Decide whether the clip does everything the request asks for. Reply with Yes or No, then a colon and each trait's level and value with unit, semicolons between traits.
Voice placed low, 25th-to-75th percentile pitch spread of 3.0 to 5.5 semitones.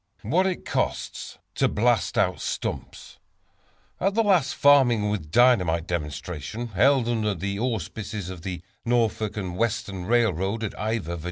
Yes: low, 110 Hz; average, 4.7 semitones